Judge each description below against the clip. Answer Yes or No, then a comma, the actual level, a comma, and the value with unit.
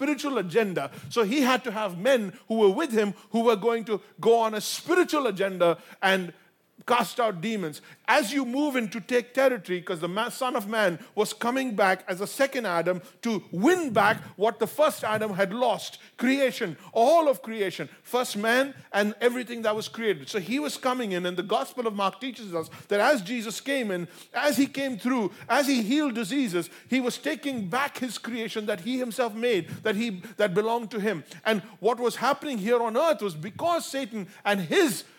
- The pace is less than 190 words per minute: No, average, 200 wpm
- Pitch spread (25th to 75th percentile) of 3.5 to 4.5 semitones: Yes, average, 4.0 semitones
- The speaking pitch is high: Yes, high, 230 Hz